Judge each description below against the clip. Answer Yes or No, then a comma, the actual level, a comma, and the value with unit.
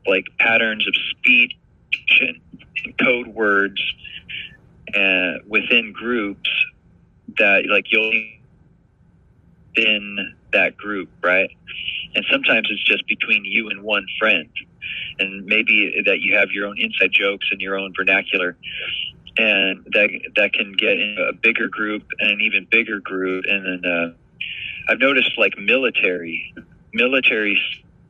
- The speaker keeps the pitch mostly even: Yes, narrow, 2.2 semitones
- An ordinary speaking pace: No, slow, 130 wpm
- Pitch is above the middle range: No, low, 100 Hz